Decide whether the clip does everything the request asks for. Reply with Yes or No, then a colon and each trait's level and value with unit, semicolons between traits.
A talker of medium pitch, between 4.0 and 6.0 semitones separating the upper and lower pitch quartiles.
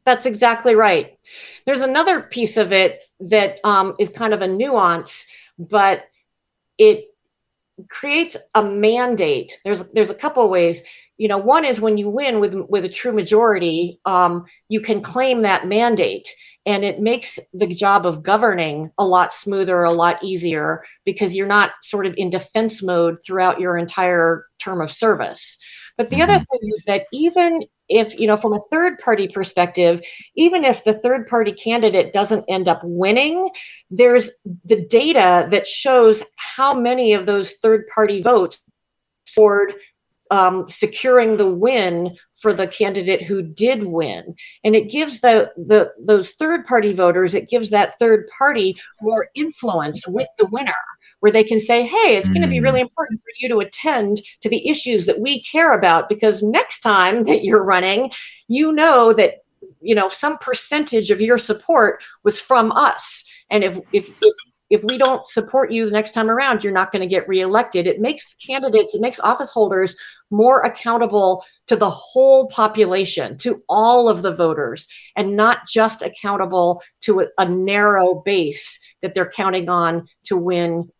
No: high, 215 Hz; average, 4.4 semitones